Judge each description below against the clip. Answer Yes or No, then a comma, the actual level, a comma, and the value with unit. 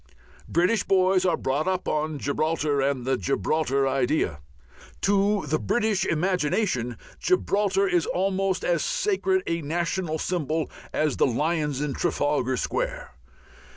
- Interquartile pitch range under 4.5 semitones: No, average, 5.2 semitones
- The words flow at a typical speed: No, slow, 125 wpm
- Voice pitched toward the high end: No, medium, 165 Hz